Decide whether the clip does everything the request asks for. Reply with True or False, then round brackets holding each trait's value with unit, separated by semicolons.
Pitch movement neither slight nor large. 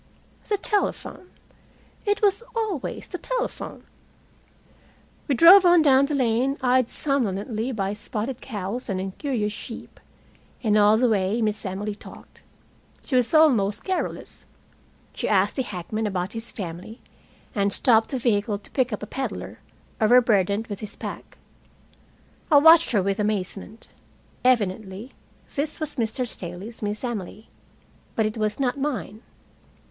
True (4.6 semitones)